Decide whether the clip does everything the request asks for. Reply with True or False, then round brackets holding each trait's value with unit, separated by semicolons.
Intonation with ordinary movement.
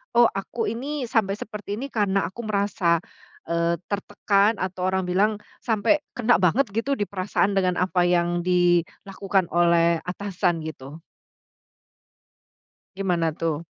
True (3.1 semitones)